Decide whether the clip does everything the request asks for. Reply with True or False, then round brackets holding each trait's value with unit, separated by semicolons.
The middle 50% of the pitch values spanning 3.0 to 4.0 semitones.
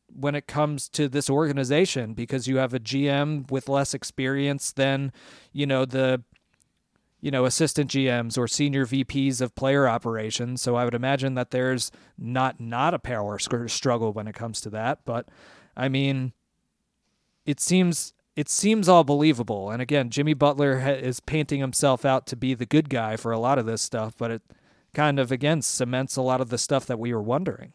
False (2.6 semitones)